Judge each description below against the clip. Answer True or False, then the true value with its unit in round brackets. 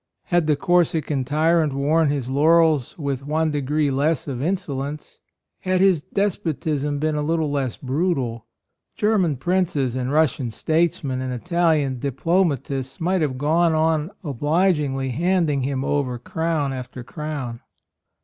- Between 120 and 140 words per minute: True (135 wpm)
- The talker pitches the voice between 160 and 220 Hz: False (150 Hz)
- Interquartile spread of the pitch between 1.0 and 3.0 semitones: False (3.5 semitones)